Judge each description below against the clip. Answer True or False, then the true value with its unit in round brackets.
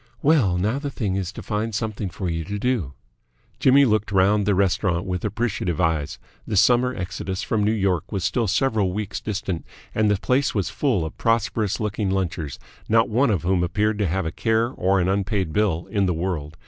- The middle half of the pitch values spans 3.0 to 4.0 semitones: True (3.3 semitones)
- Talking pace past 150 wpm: True (200 wpm)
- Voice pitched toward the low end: True (100 Hz)